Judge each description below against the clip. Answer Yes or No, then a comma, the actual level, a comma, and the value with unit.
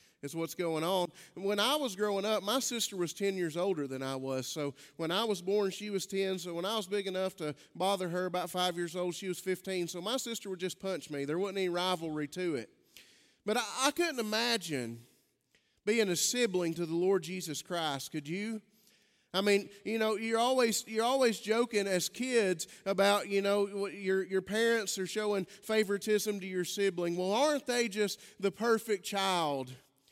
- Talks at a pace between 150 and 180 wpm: No, average, 200 wpm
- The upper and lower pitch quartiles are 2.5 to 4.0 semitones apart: Yes, average, 3.5 semitones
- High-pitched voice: Yes, high, 195 Hz